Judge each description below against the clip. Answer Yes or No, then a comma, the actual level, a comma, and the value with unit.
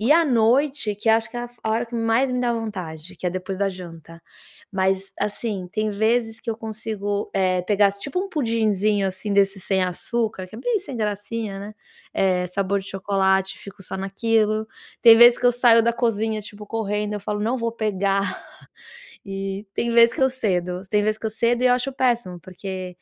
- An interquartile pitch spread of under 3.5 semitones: Yes, average, 3.1 semitones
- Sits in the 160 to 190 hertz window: No, high, 210 Hz